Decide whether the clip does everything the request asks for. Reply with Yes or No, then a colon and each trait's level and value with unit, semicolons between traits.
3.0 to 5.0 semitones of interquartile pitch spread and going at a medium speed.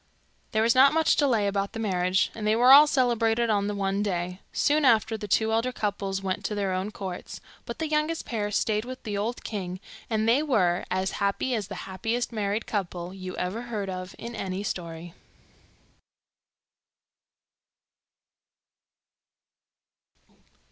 Yes: average, 3.6 semitones; average, 155 wpm